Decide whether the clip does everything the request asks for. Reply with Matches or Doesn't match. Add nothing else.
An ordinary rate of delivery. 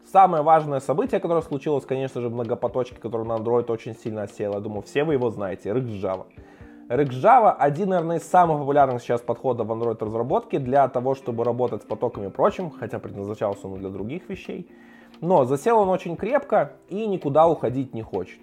Doesn't match